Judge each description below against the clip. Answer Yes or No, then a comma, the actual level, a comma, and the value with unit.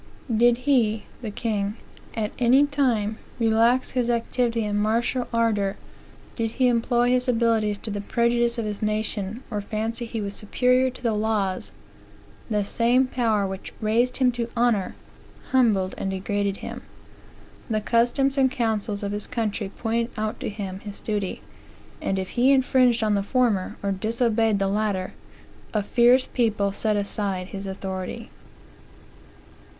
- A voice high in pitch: Yes, high, 220 Hz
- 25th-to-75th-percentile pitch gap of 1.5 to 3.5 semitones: Yes, average, 2.8 semitones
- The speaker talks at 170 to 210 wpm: No, average, 150 wpm